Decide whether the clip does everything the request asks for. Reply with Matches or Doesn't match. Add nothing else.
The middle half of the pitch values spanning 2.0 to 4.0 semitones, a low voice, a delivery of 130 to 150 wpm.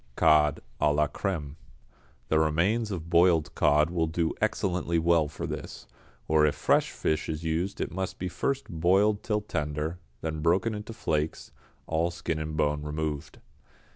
Doesn't match